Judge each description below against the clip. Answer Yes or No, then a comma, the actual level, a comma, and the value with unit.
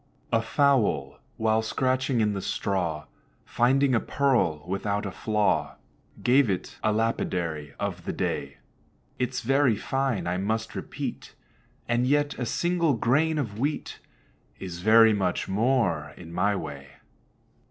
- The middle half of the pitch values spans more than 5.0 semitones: Yes, wide, 5.5 semitones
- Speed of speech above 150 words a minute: No, slow, 135 wpm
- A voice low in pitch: Yes, low, 110 Hz